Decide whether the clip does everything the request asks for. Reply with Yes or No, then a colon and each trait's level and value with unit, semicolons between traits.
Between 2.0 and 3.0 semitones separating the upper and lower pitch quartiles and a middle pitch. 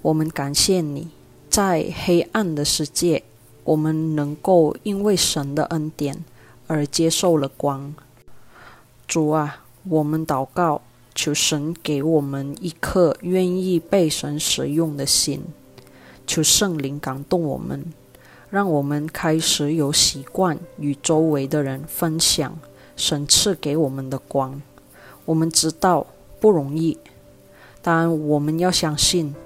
Yes: average, 2.7 semitones; medium, 155 Hz